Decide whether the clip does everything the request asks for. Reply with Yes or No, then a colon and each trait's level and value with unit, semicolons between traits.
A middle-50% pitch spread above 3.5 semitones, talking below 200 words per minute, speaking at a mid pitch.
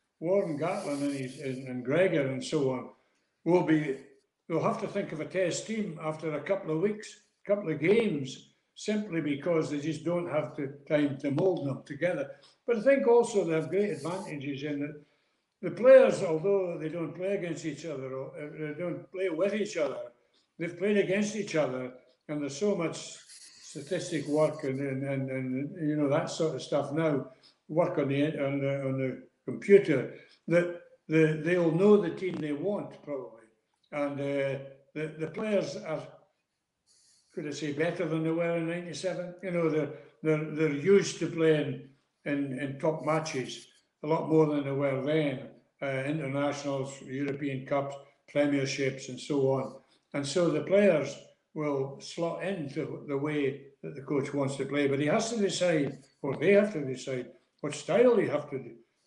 Yes: average, 3.9 semitones; average, 180 wpm; medium, 155 Hz